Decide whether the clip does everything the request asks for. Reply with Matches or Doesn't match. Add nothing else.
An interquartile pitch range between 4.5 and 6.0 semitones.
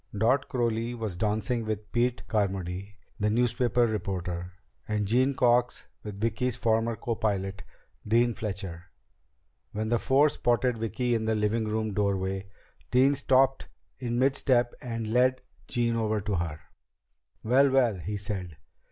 Doesn't match